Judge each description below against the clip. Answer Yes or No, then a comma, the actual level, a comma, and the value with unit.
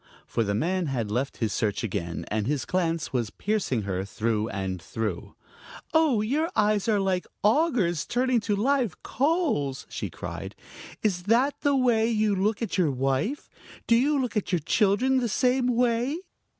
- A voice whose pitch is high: Yes, high, 205 Hz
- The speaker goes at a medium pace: Yes, average, 170 wpm